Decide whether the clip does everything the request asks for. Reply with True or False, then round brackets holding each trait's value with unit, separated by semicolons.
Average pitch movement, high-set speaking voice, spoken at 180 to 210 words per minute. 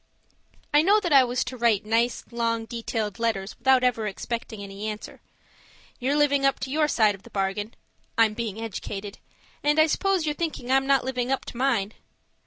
True (4.2 semitones; 235 Hz; 190 wpm)